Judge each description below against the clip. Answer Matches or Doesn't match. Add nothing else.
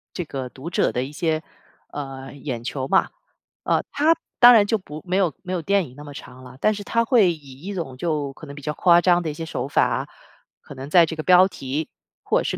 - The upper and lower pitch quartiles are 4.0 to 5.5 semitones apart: Matches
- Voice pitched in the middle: Matches